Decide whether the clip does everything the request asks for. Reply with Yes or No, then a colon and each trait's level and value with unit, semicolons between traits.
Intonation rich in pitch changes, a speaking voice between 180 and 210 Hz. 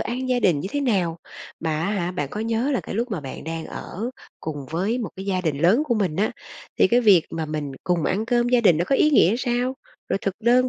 Yes: wide, 6.4 semitones; high, 200 Hz